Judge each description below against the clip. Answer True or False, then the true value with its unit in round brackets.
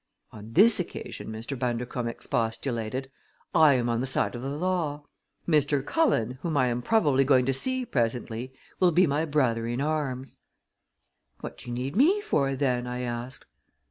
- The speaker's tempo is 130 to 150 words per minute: False (170 wpm)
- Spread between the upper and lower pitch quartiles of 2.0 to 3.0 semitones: False (4.0 semitones)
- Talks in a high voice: False (130 Hz)